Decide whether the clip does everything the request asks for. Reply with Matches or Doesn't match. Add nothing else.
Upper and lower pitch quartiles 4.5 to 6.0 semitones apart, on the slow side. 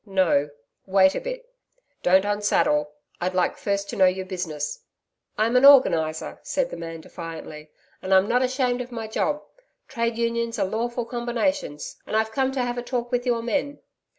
Doesn't match